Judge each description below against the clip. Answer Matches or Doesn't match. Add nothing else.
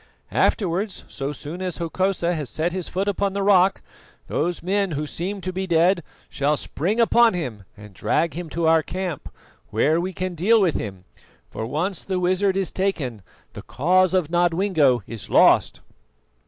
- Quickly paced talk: Doesn't match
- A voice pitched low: Doesn't match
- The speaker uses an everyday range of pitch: Matches